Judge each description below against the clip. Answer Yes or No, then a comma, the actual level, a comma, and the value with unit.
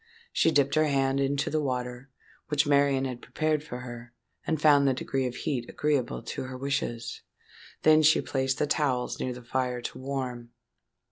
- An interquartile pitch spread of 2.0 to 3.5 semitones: Yes, narrow, 2.5 semitones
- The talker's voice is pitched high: No, low, 135 Hz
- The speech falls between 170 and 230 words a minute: Yes, average, 180 wpm